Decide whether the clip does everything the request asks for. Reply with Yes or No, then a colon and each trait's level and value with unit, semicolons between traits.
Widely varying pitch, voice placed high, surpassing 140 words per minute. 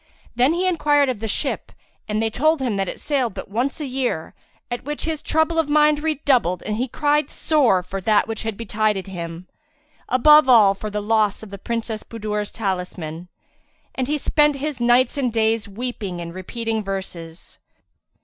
Yes: wide, 5.9 semitones; high, 225 Hz; average, 180 wpm